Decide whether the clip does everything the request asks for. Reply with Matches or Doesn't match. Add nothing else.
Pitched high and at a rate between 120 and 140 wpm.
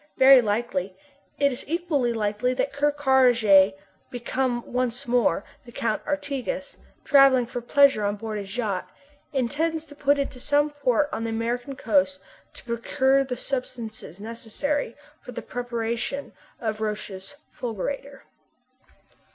Matches